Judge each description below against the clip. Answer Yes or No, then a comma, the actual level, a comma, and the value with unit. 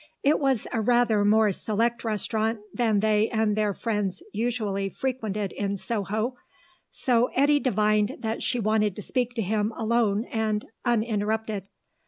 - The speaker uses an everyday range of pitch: No, narrow, 2.2 semitones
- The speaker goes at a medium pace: Yes, average, 145 wpm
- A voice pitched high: Yes, high, 220 Hz